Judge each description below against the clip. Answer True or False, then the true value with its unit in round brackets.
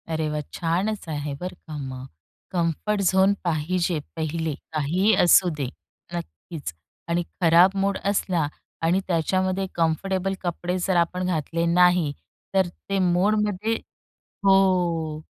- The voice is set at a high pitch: False (175 Hz)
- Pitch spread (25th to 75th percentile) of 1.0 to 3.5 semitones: True (2.8 semitones)